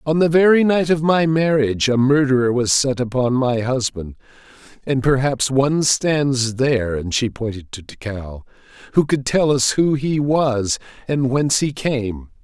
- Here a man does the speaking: Yes, male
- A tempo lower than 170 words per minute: Yes, average, 160 wpm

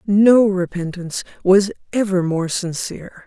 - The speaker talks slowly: Yes, slow, 110 wpm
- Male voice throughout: No, female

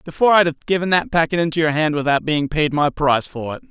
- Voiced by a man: Yes, male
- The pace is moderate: No, fast, 260 wpm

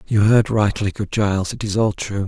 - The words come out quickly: Yes, fast, 235 wpm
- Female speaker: No, male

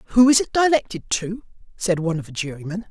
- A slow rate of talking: No, fast, 205 wpm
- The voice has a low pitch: No, high, 200 Hz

